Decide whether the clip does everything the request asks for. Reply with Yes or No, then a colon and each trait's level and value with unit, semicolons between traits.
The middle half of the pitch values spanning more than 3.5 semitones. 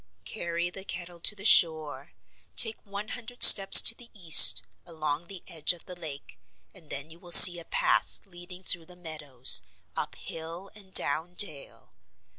No: average, 3.2 semitones